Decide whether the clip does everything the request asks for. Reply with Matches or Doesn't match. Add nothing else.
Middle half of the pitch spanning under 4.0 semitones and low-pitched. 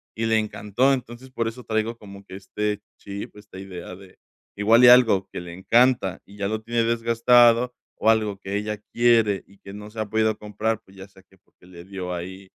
Matches